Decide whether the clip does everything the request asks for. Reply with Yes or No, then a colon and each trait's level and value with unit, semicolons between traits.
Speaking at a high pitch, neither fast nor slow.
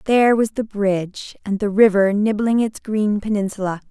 Yes: high, 210 Hz; average, 170 wpm